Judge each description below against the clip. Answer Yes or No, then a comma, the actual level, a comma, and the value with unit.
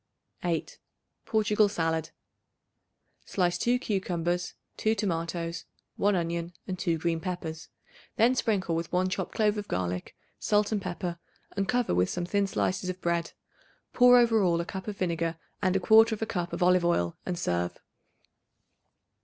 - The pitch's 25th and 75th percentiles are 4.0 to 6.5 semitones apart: No, average, 3.5 semitones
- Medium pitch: Yes, medium, 180 Hz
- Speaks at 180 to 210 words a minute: No, average, 150 wpm